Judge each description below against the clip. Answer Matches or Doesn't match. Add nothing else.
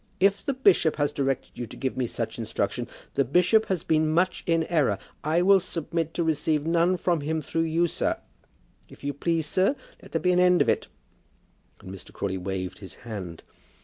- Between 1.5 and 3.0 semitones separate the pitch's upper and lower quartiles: Doesn't match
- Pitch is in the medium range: Matches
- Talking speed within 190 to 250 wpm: Matches